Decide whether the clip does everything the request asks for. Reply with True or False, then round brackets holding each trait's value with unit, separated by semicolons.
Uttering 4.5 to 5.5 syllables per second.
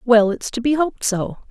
True (5.4 syllables/s)